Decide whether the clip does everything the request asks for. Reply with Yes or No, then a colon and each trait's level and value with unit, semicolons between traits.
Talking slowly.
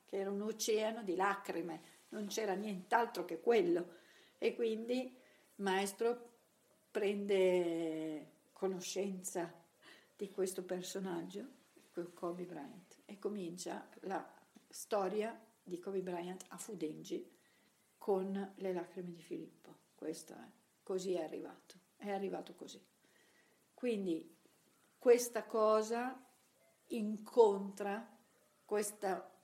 Yes: slow, 100 wpm